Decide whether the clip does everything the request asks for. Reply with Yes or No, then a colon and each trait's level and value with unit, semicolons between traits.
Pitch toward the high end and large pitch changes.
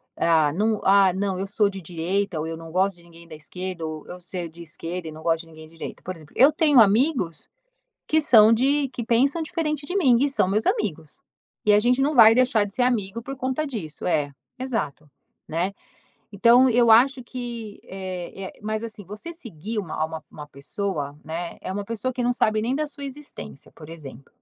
Yes: high, 200 Hz; wide, 6.8 semitones